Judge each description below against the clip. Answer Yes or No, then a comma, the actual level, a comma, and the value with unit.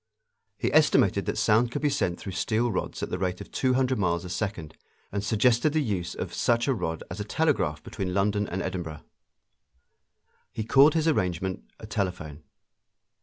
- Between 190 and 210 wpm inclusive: No, average, 180 wpm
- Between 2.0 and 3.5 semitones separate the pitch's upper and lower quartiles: No, average, 5.2 semitones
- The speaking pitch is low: Yes, low, 100 Hz